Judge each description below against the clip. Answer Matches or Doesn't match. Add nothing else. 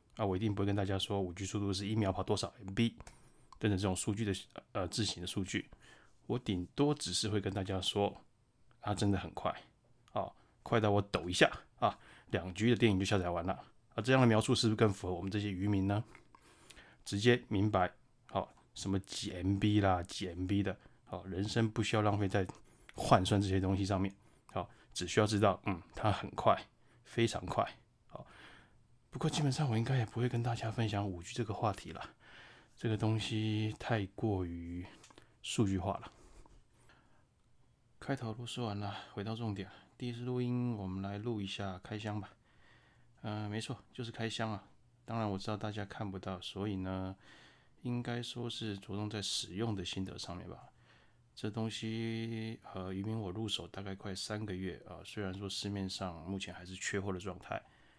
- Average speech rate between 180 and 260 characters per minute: Doesn't match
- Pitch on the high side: Doesn't match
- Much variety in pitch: Doesn't match